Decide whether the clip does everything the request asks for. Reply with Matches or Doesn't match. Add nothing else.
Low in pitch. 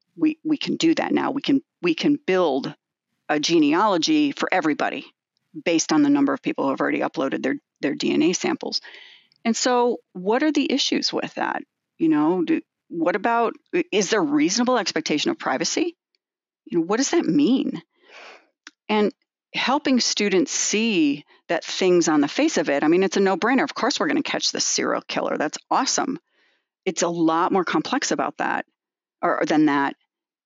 Doesn't match